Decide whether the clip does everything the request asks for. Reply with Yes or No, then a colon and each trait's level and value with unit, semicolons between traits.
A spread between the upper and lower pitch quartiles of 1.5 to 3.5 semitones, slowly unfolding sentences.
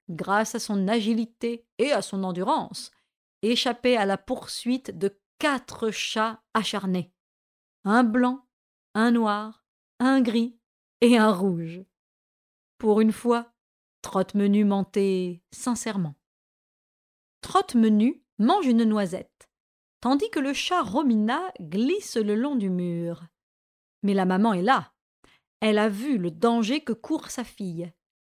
No: average, 3.9 semitones; slow, 125 wpm